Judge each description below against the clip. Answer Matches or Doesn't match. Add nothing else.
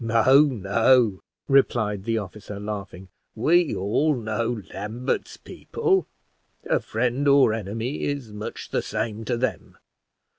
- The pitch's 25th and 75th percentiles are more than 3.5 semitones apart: Matches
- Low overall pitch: Matches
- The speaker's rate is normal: Doesn't match